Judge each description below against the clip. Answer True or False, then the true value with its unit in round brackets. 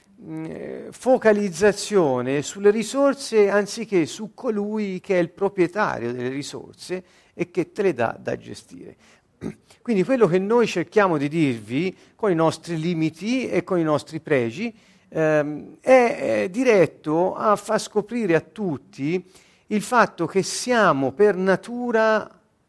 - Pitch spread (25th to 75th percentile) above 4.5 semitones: True (5.0 semitones)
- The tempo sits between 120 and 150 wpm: True (125 wpm)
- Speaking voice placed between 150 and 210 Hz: True (190 Hz)